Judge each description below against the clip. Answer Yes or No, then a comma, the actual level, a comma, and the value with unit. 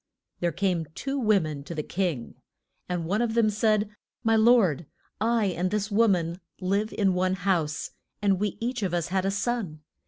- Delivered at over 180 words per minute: Yes, average, 190 wpm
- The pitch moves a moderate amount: Yes, average, 3.8 semitones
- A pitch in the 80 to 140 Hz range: No, high, 195 Hz